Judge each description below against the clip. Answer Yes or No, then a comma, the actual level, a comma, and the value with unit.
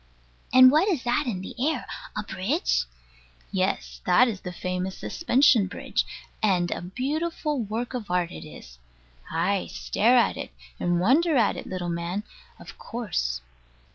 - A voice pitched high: Yes, high, 210 Hz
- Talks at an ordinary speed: Yes, average, 155 wpm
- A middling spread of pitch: No, wide, 6.3 semitones